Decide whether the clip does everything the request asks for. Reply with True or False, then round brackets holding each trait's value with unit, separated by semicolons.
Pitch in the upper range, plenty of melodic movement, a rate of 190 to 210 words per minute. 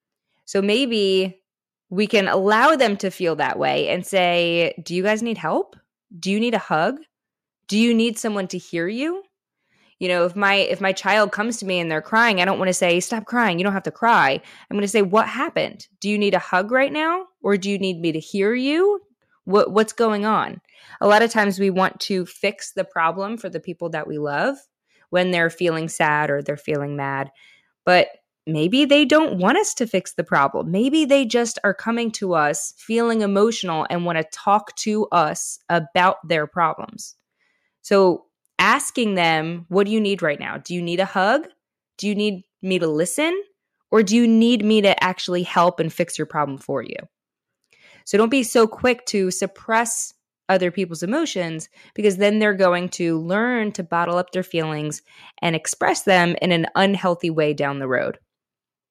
False (195 Hz; 4.3 semitones; 200 wpm)